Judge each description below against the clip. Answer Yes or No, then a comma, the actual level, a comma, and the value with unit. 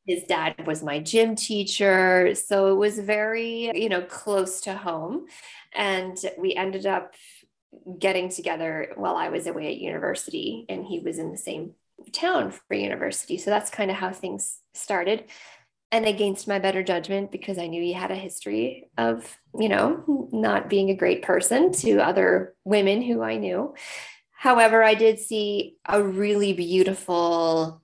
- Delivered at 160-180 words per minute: Yes, average, 165 wpm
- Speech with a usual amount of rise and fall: Yes, average, 3.3 semitones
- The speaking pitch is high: Yes, high, 195 Hz